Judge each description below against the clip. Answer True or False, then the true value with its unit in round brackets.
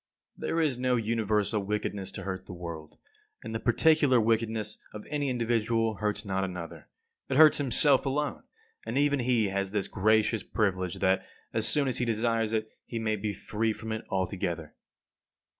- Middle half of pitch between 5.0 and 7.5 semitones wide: False (3.5 semitones)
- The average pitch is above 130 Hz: False (110 Hz)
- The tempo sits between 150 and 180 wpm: True (175 wpm)